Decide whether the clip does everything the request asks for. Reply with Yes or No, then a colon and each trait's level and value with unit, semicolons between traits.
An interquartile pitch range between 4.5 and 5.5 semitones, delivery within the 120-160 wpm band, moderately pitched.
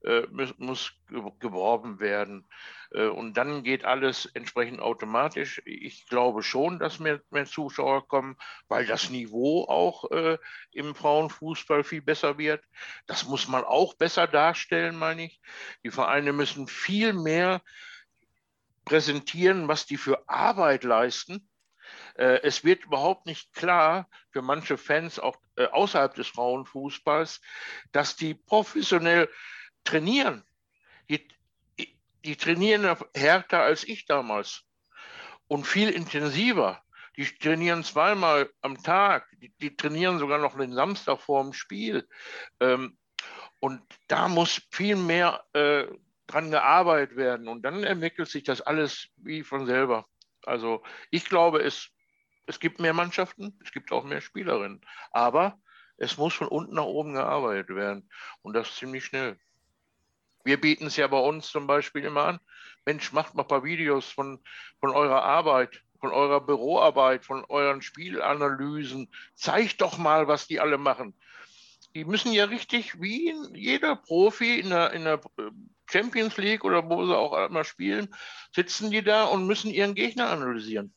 Yes: average, 4.9 semitones; average, 140 wpm; medium, 150 Hz